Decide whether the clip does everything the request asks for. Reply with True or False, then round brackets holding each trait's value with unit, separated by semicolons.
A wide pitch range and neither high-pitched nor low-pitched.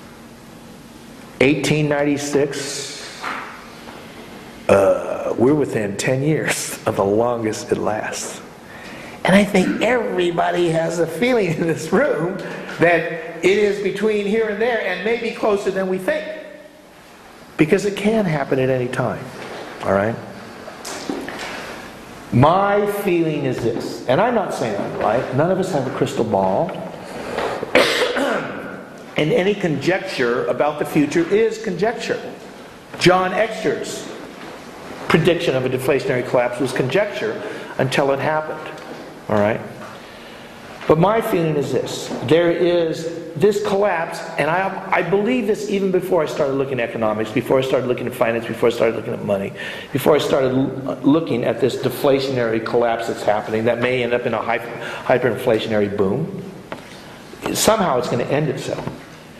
True (7.0 semitones; 165 Hz)